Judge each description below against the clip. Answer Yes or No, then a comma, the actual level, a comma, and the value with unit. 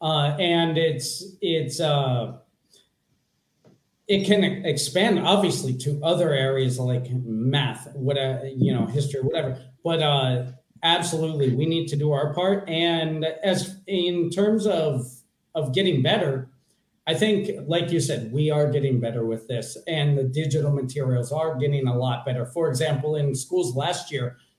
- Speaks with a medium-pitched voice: Yes, medium, 150 Hz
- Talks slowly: No, average, 150 wpm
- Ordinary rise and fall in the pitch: Yes, average, 4.2 semitones